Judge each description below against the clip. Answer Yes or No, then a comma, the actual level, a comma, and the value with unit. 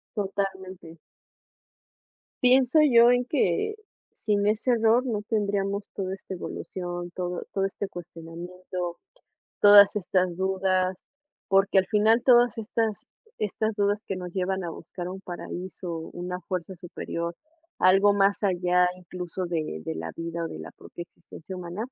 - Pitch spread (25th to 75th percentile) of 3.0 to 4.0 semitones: No, narrow, 2.6 semitones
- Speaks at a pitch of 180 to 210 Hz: Yes, high, 190 Hz